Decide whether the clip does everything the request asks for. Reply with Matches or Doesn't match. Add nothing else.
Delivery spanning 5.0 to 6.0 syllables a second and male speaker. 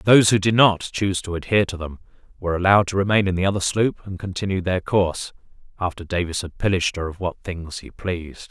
Doesn't match